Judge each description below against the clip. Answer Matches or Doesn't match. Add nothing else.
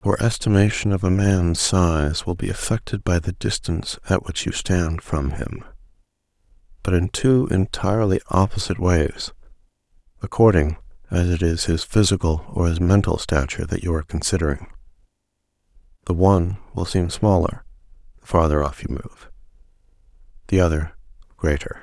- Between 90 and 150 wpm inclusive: Matches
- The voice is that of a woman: Doesn't match